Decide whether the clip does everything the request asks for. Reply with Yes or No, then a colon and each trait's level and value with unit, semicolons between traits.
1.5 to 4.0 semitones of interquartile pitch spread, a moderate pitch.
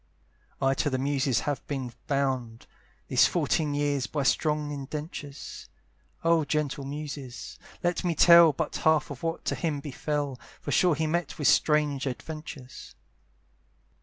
Yes: narrow, 2.4 semitones; medium, 145 Hz